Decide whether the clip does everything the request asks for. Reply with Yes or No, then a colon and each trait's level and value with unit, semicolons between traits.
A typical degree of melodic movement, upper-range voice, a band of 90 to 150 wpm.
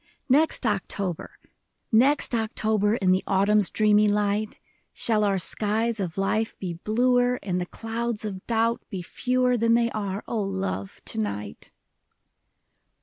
Yes: average, 3.0 semitones; high, 210 Hz; average, 140 wpm